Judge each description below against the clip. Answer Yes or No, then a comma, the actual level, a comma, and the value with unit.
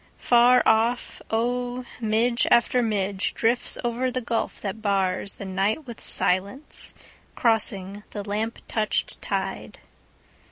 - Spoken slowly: Yes, slow, 110 wpm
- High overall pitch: Yes, high, 225 Hz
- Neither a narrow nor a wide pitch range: Yes, average, 3.2 semitones